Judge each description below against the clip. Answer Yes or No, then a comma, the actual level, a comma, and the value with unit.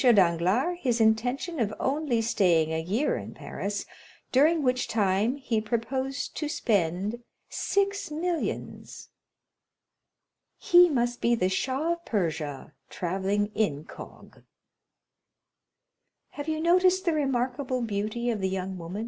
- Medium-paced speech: No, slow, 125 wpm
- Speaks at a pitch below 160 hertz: No, high, 235 Hz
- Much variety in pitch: Yes, wide, 6.7 semitones